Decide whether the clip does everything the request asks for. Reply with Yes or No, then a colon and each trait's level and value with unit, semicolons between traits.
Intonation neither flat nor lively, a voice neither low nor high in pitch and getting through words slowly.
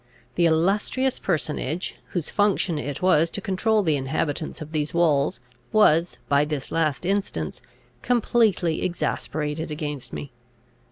Yes: average, 4.3 semitones; medium, 165 Hz; slow, 125 wpm